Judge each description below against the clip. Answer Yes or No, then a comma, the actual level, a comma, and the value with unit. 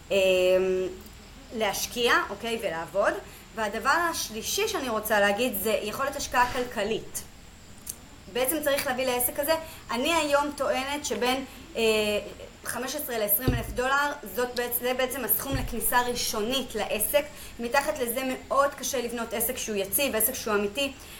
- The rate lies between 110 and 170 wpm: Yes, average, 130 wpm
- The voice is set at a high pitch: Yes, high, 245 Hz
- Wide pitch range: No, average, 4.3 semitones